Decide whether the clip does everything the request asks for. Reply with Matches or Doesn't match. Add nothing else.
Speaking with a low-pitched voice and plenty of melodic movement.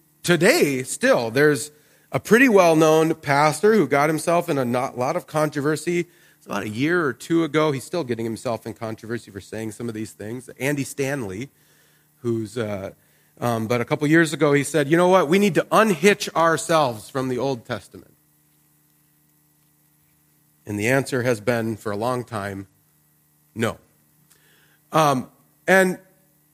Matches